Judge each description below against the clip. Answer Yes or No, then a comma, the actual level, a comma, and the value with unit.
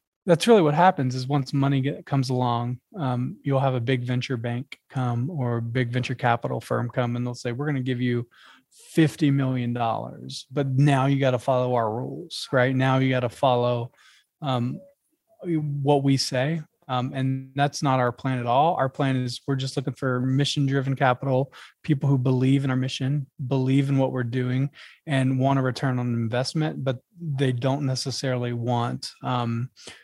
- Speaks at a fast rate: No, average, 185 wpm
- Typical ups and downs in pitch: No, narrow, 2.0 semitones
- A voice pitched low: Yes, low, 130 Hz